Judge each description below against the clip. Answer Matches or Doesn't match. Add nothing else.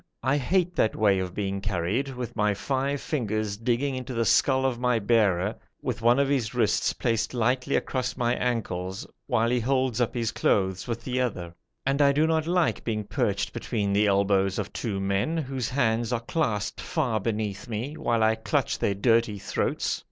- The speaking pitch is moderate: Doesn't match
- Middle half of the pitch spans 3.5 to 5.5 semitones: Matches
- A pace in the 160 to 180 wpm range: Doesn't match